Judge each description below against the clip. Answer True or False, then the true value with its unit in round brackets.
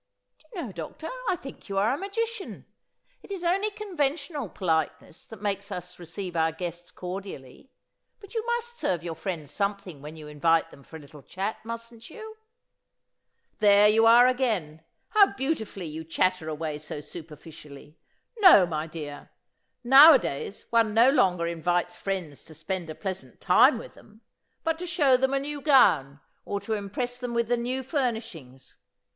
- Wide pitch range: True (8.5 semitones)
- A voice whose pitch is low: False (200 Hz)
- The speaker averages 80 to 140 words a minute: False (165 wpm)